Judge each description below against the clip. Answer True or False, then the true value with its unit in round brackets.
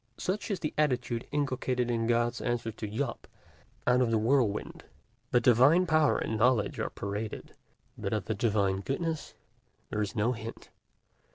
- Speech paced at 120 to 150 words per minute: False (160 wpm)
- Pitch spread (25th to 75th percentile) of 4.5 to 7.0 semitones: False (3.4 semitones)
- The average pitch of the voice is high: False (120 Hz)